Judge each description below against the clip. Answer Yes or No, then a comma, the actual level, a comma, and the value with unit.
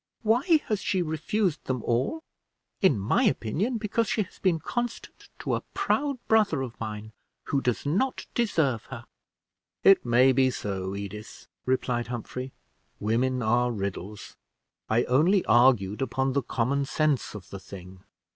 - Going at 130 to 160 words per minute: Yes, average, 150 wpm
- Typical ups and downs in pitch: No, wide, 9.0 semitones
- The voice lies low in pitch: Yes, low, 130 Hz